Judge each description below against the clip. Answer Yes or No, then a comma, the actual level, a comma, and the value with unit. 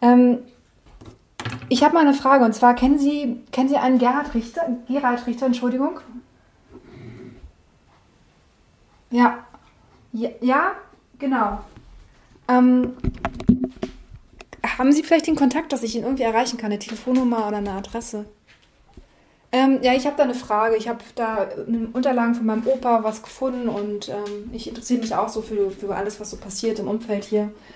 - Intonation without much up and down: No, average, 3.1 semitones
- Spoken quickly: No, average, 160 wpm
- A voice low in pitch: No, high, 245 Hz